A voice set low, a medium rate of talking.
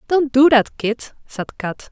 No: very high, 255 Hz; average, 190 wpm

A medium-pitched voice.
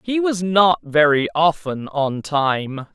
Yes: medium, 165 Hz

